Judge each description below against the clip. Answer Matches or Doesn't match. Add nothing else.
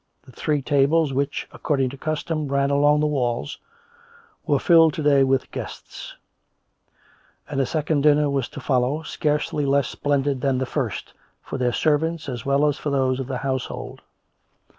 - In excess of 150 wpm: Matches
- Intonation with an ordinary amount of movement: Doesn't match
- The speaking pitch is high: Doesn't match